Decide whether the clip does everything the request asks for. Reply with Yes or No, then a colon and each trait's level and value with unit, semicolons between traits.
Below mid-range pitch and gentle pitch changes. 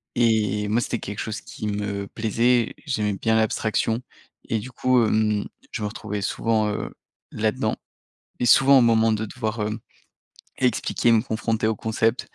Yes: low, 110 Hz; narrow, 1.7 semitones